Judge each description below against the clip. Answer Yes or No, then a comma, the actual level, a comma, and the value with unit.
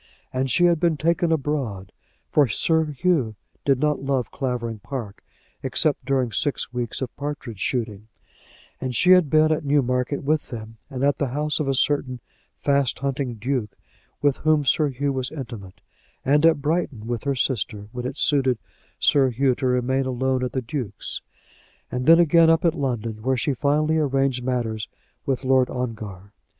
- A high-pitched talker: No, low, 135 Hz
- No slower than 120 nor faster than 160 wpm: No, average, 170 wpm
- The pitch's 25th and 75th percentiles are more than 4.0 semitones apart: No, average, 3.3 semitones